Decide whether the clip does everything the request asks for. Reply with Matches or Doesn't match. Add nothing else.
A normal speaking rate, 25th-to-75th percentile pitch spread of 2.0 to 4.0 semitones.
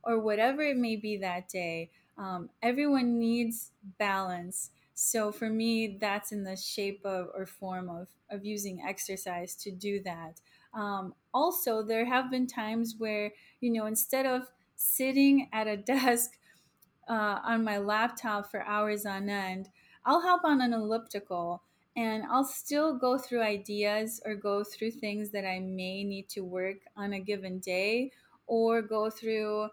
Matches